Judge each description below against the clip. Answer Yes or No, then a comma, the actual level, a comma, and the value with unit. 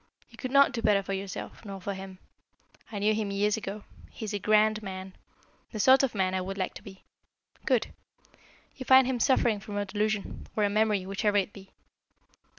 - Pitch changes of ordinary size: No, narrow, 1.9 semitones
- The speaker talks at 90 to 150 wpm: No, fast, 205 wpm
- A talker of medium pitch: No, high, 205 Hz